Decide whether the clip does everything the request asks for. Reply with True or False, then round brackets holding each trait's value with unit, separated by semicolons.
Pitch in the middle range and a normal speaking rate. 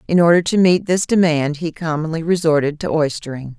True (160 Hz; 185 wpm)